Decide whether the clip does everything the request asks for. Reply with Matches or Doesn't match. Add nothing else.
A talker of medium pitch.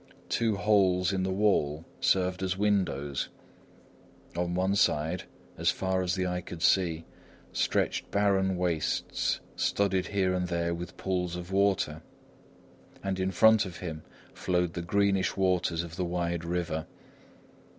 Doesn't match